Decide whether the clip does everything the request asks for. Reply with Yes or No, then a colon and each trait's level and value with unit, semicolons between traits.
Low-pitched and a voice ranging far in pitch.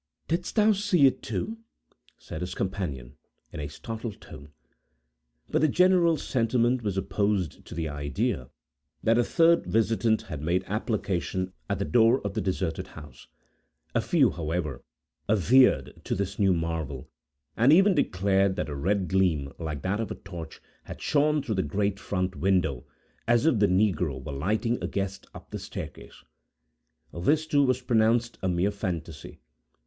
Yes: low, 100 Hz; wide, 5.8 semitones